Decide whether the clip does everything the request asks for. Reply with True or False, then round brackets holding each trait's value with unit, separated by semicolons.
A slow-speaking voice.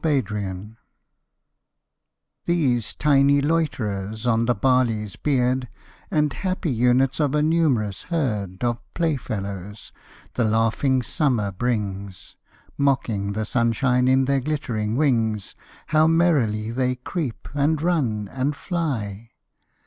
True (110 wpm)